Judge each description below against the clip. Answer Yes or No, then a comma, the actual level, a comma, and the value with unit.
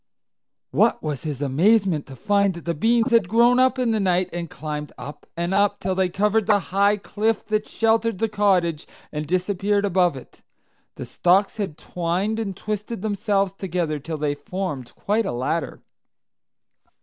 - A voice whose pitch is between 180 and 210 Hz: Yes, high, 190 Hz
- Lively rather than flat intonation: No, average, 3.9 semitones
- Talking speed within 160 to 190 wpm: Yes, average, 165 wpm